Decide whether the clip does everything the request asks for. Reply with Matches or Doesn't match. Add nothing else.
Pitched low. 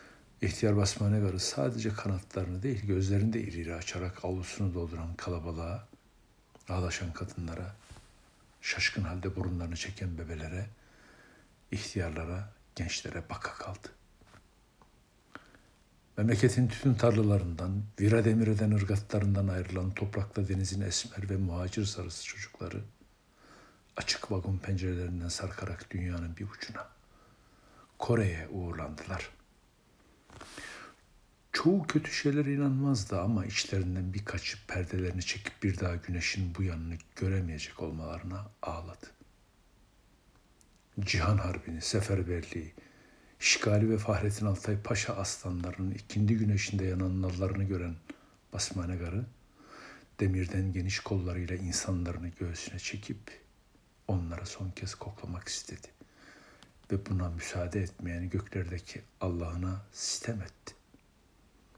Matches